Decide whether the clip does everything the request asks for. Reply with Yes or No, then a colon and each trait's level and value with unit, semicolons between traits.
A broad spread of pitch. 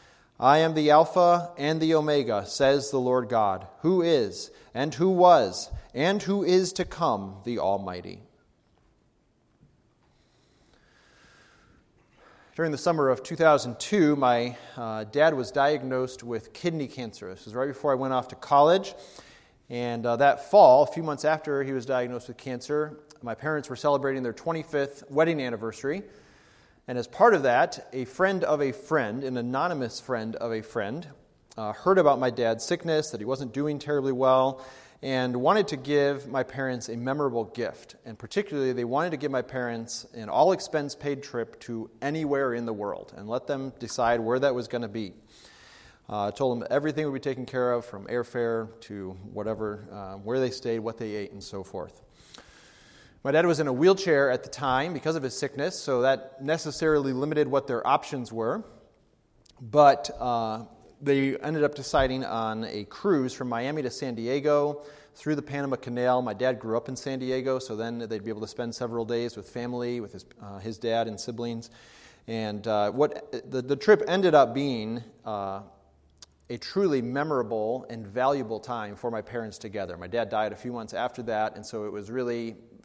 No: average, 3.9 semitones